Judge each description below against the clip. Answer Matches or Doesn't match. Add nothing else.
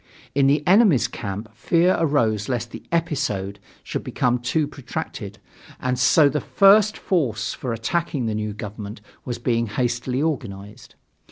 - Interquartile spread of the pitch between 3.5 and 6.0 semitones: Matches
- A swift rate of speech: Doesn't match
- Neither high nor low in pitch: Doesn't match